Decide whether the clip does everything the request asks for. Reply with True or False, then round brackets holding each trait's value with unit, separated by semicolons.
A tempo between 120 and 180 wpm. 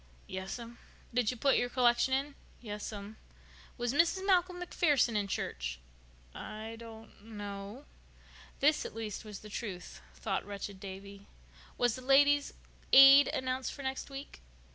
True (140 wpm)